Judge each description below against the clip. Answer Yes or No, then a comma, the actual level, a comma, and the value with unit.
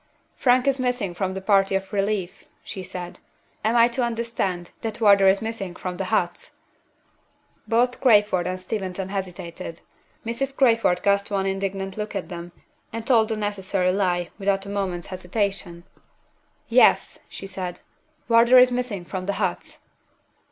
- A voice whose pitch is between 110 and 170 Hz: No, high, 195 Hz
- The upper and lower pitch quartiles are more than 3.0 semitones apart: Yes, average, 3.6 semitones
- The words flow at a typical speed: Yes, average, 150 wpm